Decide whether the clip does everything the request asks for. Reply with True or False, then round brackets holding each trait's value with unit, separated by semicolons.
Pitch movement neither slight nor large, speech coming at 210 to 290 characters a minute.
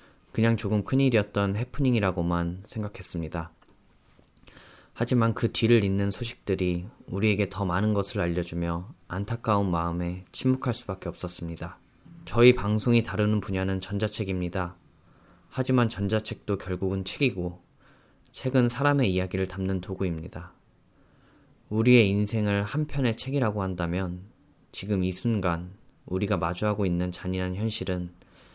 False (3.9 semitones; 310 characters per minute)